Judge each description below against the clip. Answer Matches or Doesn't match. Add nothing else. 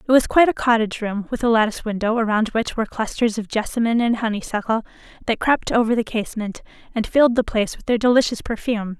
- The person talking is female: Matches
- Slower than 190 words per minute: Doesn't match